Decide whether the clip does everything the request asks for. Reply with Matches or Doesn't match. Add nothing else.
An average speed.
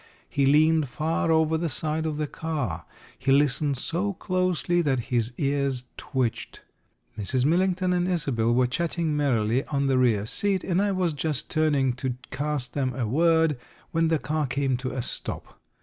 Matches